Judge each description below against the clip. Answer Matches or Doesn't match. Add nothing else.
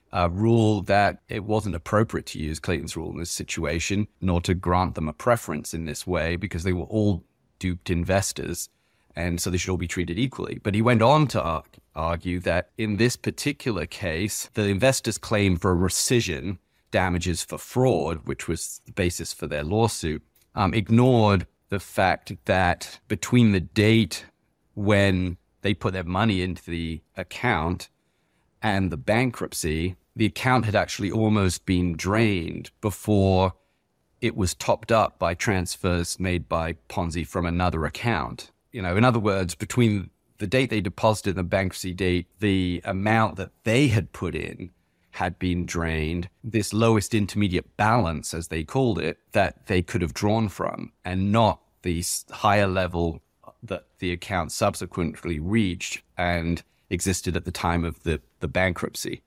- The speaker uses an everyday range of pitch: Matches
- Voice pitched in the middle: Doesn't match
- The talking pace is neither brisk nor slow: Matches